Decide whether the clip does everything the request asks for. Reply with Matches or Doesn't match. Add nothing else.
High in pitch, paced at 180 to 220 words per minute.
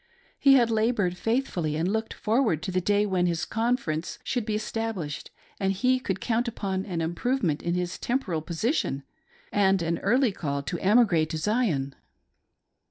Doesn't match